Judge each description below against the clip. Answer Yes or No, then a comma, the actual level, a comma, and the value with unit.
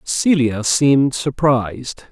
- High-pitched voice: No, low, 135 Hz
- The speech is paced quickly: No, slow, 85 wpm